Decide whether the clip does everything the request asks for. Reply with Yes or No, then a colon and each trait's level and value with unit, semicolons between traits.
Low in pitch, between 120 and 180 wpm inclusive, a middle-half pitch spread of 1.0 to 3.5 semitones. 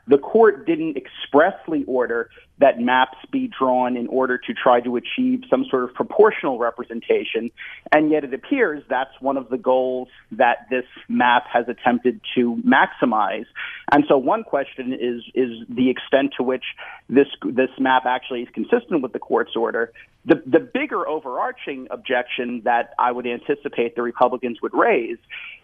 Yes: low, 130 Hz; average, 160 wpm; average, 2.7 semitones